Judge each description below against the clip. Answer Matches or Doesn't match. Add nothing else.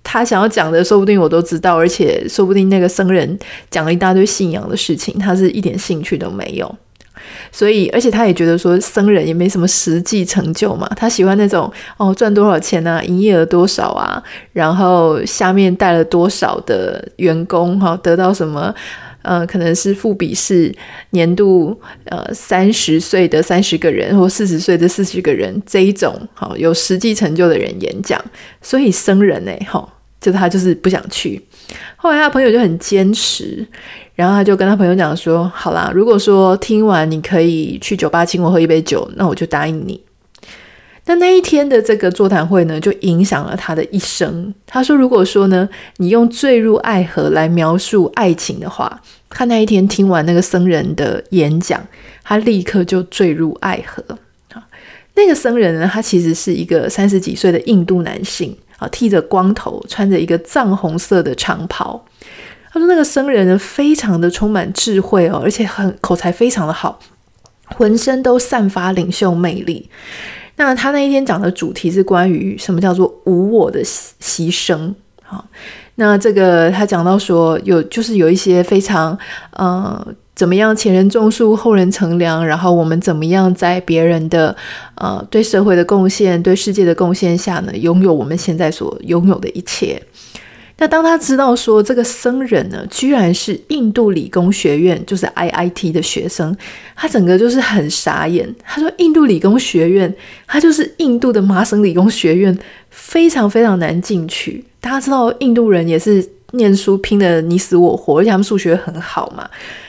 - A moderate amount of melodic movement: Matches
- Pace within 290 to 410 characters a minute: Doesn't match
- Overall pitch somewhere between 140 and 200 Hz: Matches